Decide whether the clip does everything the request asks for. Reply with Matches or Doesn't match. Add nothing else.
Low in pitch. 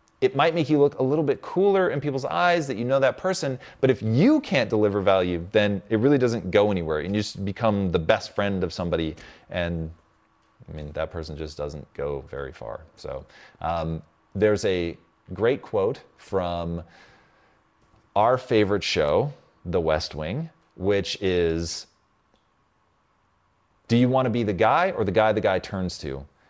Matches